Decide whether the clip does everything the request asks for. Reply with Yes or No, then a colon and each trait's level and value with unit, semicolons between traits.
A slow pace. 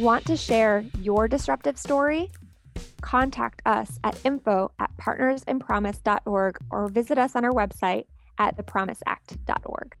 Yes: slow, 115 wpm